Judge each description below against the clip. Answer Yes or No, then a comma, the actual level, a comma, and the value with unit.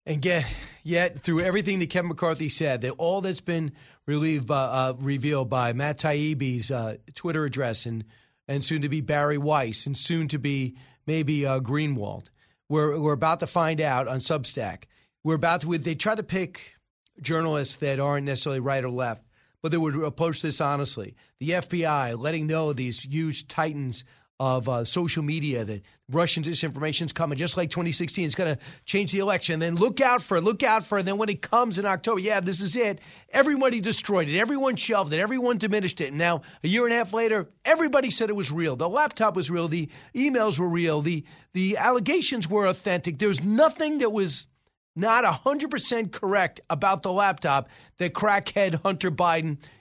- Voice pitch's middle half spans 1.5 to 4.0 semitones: No, wide, 5.4 semitones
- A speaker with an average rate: Yes, average, 195 wpm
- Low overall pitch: No, medium, 165 Hz